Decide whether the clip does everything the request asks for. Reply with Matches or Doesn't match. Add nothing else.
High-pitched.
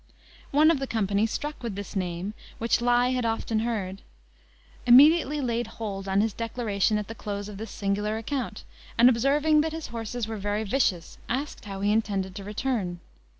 Matches